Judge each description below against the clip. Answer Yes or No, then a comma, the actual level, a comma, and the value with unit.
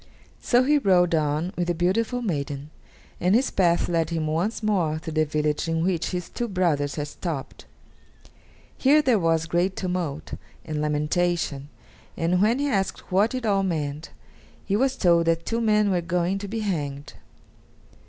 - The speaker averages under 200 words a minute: Yes, average, 170 wpm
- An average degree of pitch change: Yes, average, 4.5 semitones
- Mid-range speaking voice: Yes, medium, 175 Hz